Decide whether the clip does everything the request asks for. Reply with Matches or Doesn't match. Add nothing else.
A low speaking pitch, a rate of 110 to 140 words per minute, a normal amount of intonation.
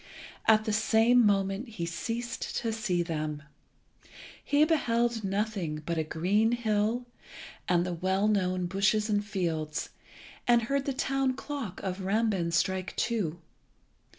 Doesn't match